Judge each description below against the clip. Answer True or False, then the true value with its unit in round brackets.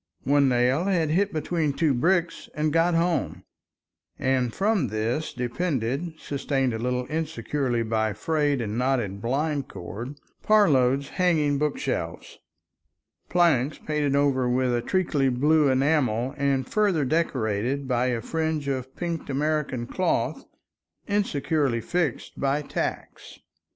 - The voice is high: False (140 Hz)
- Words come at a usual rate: False (125 wpm)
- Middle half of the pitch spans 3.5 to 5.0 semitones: True (4.2 semitones)